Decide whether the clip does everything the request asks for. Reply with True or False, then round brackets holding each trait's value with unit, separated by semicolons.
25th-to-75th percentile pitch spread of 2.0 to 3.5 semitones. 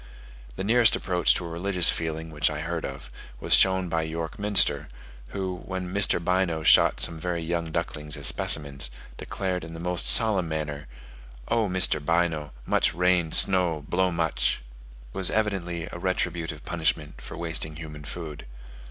True (2.7 semitones)